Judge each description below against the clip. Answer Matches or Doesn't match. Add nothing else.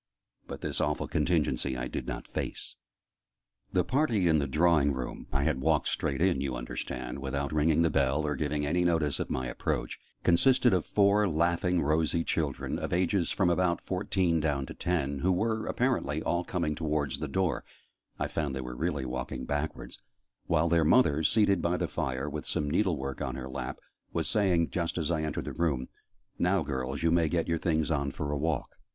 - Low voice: Matches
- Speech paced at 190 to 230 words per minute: Matches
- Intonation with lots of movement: Doesn't match